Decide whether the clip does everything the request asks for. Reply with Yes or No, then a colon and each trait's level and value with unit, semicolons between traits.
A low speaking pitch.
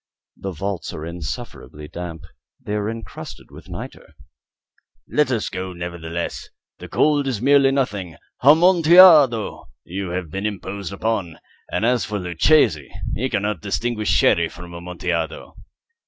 Yes: low, 100 Hz